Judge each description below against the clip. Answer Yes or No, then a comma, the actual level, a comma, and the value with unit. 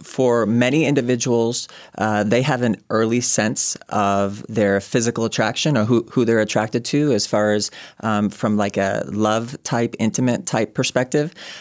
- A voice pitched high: No, low, 115 Hz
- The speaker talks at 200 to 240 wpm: No, average, 160 wpm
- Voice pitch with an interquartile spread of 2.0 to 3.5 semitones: Yes, average, 2.7 semitones